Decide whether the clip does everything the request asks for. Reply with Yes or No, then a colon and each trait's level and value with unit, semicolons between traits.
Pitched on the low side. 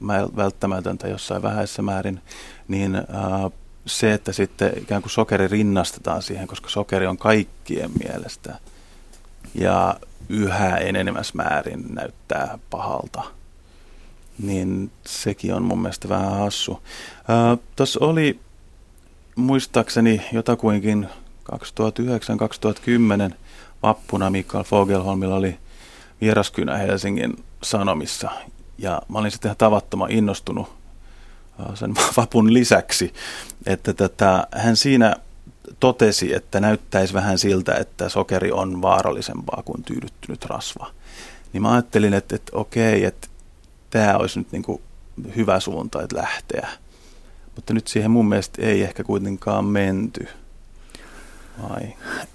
Yes: low, 100 Hz